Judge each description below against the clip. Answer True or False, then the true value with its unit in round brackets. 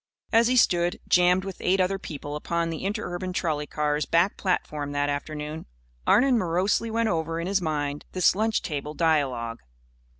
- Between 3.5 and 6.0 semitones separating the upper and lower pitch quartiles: True (4.2 semitones)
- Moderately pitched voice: True (170 Hz)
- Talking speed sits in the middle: True (165 wpm)